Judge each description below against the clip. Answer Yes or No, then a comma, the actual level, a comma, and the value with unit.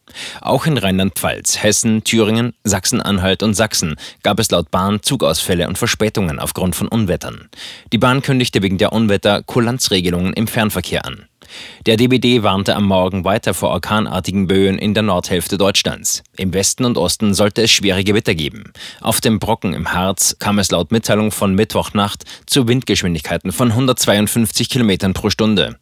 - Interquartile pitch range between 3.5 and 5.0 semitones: No, average, 3.1 semitones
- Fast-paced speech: No, average, 160 wpm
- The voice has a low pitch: Yes, low, 105 Hz